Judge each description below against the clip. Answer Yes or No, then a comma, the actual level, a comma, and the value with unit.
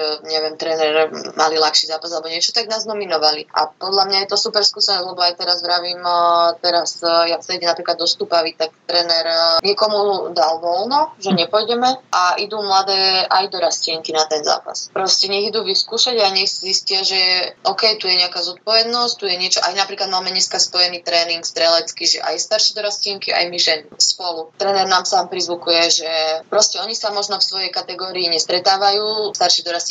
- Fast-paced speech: Yes, fast, 180 wpm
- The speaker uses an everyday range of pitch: Yes, average, 3.0 semitones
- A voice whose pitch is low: No, medium, 180 Hz